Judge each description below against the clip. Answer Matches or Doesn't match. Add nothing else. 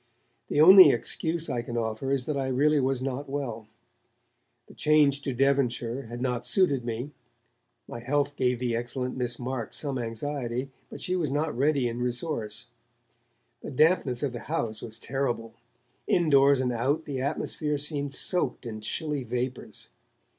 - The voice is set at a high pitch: Doesn't match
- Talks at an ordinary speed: Matches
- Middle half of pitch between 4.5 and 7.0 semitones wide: Doesn't match